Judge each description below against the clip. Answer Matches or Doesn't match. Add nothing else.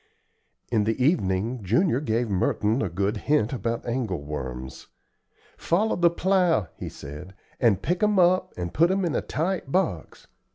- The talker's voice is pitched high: Doesn't match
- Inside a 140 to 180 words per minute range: Matches